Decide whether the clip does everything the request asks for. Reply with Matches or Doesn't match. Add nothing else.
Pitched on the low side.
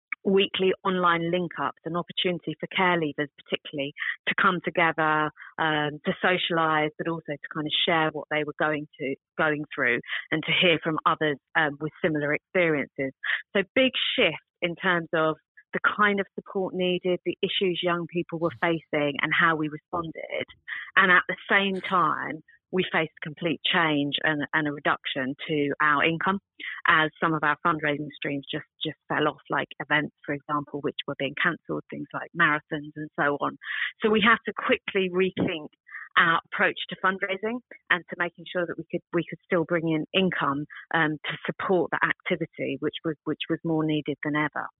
Doesn't match